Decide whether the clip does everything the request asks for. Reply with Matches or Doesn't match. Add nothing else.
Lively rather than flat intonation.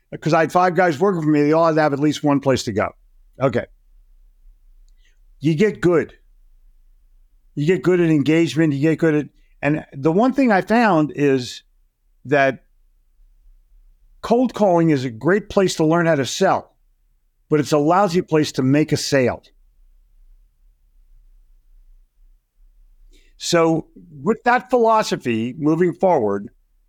Matches